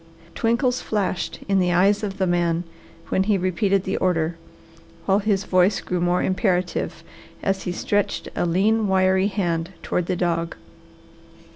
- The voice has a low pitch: No, high, 190 Hz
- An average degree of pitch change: No, narrow, 2.1 semitones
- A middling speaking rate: Yes, average, 150 wpm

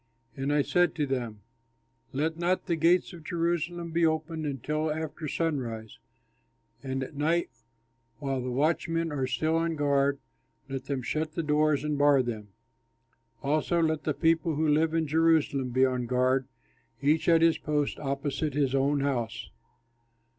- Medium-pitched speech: Yes, medium, 150 Hz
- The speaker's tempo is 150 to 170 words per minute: Yes, average, 155 wpm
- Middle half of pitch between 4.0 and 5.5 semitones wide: No, average, 3.1 semitones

